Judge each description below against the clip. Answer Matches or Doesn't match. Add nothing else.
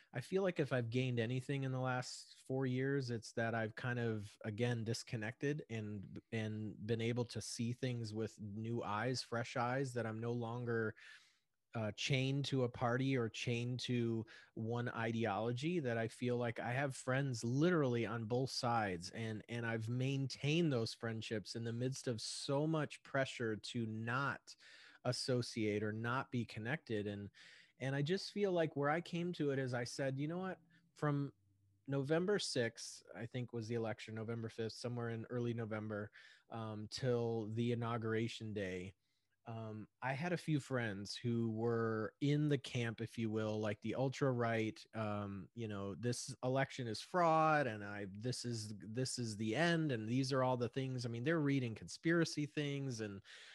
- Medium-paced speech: Matches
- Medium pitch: Doesn't match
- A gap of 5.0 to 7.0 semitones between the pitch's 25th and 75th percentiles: Doesn't match